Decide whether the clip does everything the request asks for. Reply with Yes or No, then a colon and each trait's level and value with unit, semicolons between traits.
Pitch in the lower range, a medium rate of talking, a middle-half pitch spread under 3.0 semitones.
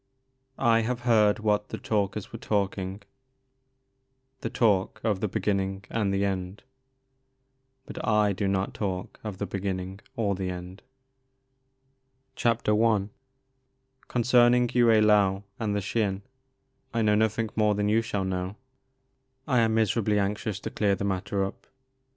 Yes: low, 105 Hz; average, 145 wpm; narrow, 2.4 semitones